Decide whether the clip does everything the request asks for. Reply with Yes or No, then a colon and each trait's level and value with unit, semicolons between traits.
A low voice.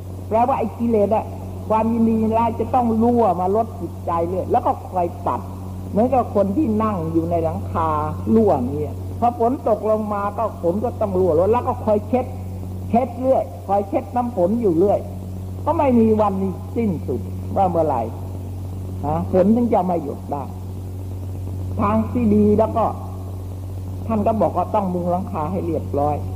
Yes: very low, 95 Hz